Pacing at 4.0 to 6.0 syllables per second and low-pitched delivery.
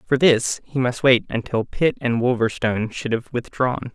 Yes: 4.7 syllables/s; low, 125 Hz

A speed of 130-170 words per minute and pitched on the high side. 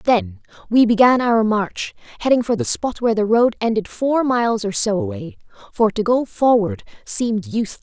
No: average, 185 wpm; high, 235 Hz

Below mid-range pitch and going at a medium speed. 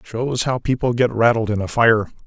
No: low, 115 Hz; fast, 210 wpm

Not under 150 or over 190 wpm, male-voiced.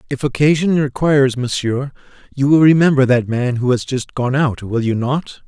Yes: average, 185 wpm; male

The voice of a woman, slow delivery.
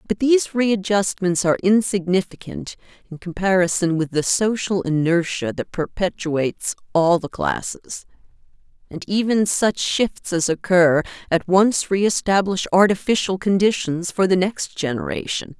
Yes: female; slow, 120 wpm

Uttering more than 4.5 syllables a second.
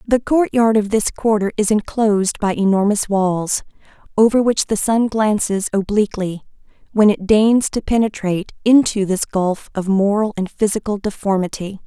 Yes: 4.9 syllables/s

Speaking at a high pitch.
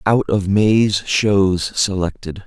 No: low, 100 Hz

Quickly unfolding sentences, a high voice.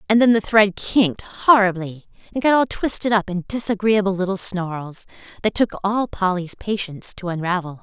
No: average, 170 wpm; high, 200 Hz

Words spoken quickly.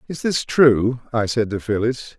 No: average, 190 wpm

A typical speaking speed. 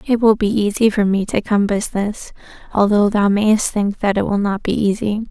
No: fast, 215 wpm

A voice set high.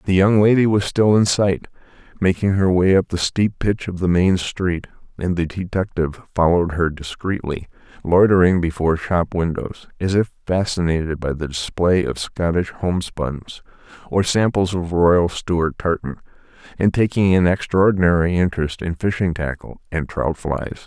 No: very low, 90 Hz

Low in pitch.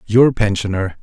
Yes: low, 105 Hz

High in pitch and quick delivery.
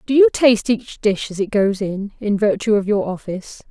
Yes: high, 210 Hz; fast, 225 wpm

